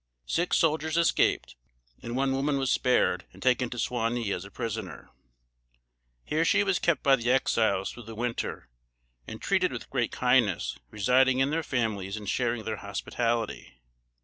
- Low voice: Yes, low, 120 Hz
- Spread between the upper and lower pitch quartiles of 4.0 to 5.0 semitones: No, average, 3.6 semitones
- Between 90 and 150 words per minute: No, average, 160 wpm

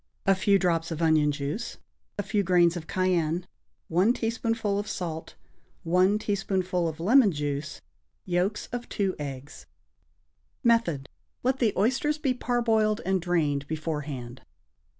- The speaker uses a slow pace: Yes, slow, 130 wpm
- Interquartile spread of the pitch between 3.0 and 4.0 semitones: No, average, 5.0 semitones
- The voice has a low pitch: No, medium, 185 Hz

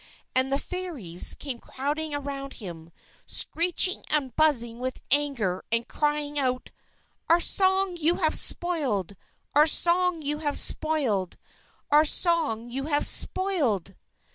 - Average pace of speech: No, slow, 125 wpm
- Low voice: No, very high, 290 Hz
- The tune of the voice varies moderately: Yes, average, 4.8 semitones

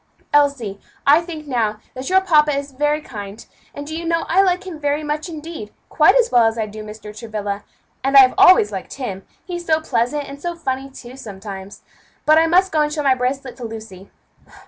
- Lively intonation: Yes, wide, 6.1 semitones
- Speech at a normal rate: No, fast, 210 wpm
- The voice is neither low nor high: No, very high, 275 Hz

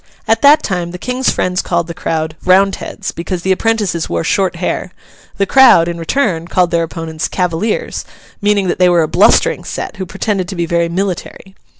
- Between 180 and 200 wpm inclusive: Yes, average, 190 wpm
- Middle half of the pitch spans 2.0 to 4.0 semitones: Yes, average, 2.8 semitones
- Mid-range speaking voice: Yes, medium, 180 Hz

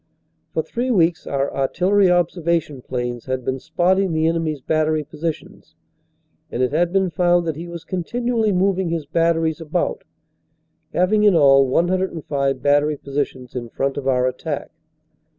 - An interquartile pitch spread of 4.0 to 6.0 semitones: Yes, average, 4.4 semitones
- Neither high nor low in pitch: Yes, medium, 160 Hz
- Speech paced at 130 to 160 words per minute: Yes, average, 150 wpm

